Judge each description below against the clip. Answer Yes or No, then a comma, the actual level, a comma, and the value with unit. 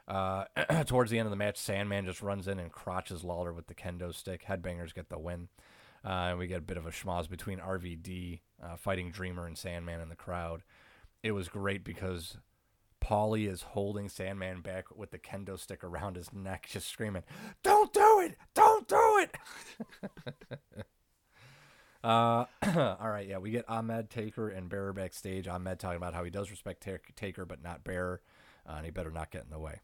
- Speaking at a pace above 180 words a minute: Yes, average, 195 wpm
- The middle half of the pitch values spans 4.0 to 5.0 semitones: No, average, 2.7 semitones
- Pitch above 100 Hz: No, very low, 95 Hz